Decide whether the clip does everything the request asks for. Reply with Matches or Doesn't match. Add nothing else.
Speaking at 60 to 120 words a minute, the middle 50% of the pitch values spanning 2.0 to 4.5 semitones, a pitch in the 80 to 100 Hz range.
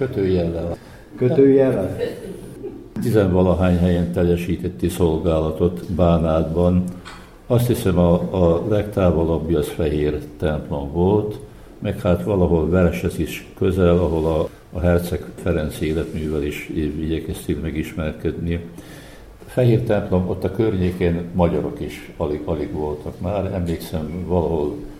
Matches